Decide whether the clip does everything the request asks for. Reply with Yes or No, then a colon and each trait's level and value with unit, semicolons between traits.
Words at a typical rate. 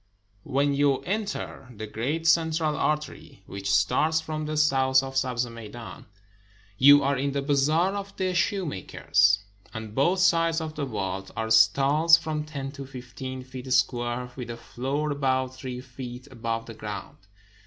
Yes: average, 160 wpm